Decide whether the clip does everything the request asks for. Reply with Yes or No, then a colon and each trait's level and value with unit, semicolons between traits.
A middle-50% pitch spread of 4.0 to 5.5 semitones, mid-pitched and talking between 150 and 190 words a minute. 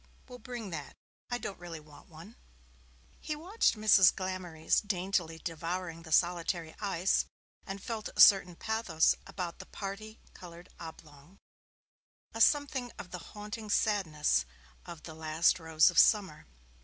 No: average, 4.4 semitones; medium, 180 Hz; average, 140 wpm